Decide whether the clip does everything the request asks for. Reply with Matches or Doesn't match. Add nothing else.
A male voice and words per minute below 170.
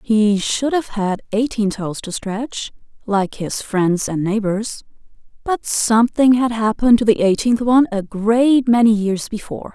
Doesn't match